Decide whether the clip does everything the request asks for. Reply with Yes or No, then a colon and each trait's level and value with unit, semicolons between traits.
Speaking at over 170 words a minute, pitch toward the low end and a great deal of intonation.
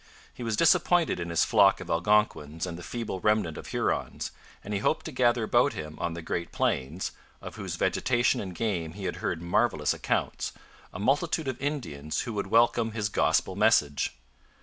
Yes: average, 185 wpm; low, 105 Hz; wide, 6.1 semitones